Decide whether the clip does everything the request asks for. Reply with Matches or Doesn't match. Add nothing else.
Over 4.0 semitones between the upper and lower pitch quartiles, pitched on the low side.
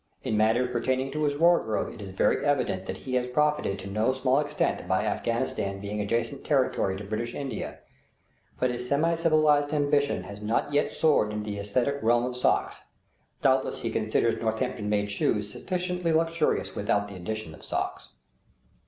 Matches